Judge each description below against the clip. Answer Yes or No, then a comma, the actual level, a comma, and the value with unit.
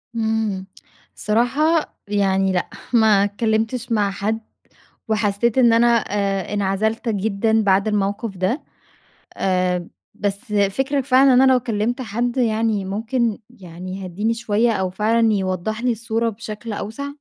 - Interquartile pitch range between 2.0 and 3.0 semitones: Yes, average, 2.7 semitones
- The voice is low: No, high, 215 Hz